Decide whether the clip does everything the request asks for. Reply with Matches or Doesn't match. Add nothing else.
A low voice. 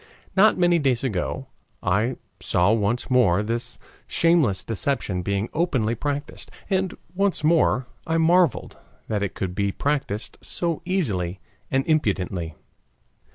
Matches